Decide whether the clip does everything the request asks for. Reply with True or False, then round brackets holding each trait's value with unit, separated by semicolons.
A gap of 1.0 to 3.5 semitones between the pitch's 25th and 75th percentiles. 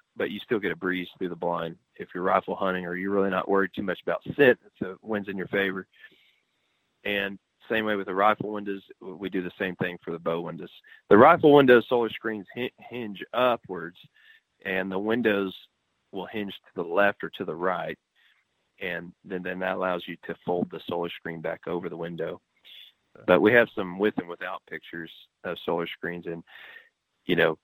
True (2.9 semitones)